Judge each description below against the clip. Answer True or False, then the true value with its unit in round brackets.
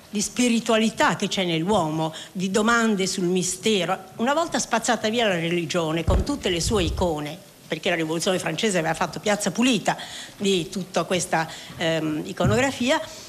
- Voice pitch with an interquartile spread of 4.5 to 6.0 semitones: True (4.9 semitones)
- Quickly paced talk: False (150 wpm)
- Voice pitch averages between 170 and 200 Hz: True (190 Hz)